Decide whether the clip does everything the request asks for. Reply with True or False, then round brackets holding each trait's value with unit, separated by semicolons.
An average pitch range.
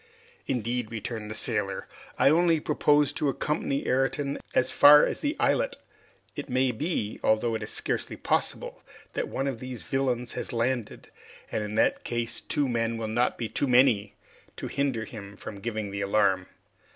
True (4.1 semitones)